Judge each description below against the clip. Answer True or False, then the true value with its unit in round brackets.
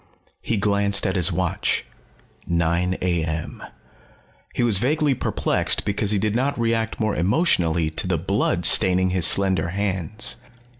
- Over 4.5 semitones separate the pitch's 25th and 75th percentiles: False (3.7 semitones)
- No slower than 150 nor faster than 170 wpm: False (140 wpm)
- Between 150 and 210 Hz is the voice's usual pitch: False (100 Hz)